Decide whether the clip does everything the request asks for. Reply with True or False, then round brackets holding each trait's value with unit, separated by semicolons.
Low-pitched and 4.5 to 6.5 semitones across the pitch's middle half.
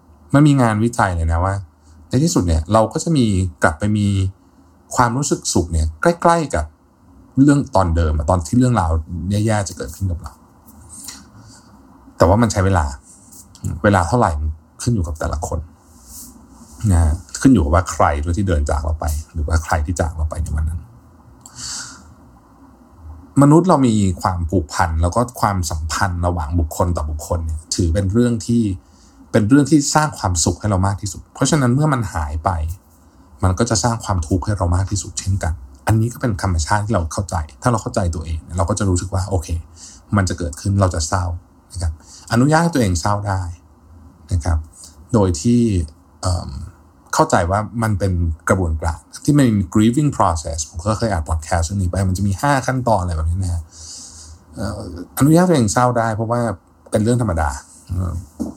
True (95 Hz; 4.9 semitones)